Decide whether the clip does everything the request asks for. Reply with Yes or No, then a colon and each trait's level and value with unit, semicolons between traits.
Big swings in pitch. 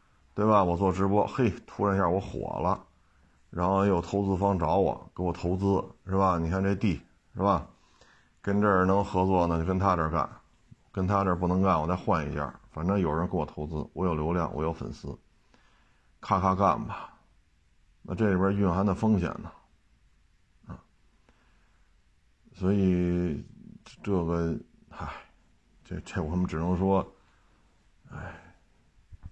No: average, 2.8 semitones